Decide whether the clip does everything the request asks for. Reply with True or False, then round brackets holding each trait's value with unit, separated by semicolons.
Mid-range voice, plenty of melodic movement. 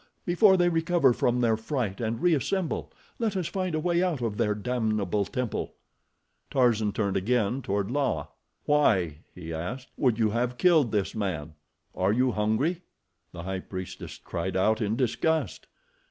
False (115 Hz; 6.5 semitones)